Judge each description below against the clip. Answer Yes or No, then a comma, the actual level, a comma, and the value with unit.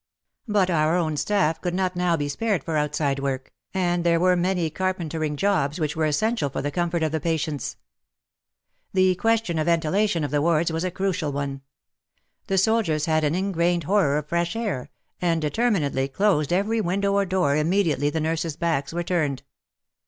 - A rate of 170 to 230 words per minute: Yes, average, 180 wpm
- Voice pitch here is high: No, medium, 170 Hz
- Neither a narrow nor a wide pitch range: Yes, average, 3.7 semitones